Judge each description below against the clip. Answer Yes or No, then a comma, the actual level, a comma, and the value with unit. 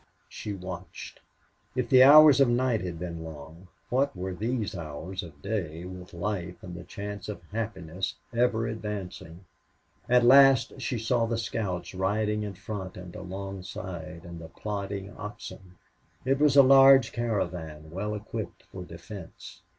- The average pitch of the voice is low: Yes, low, 100 Hz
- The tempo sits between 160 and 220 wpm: No, average, 150 wpm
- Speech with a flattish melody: No, average, 4.3 semitones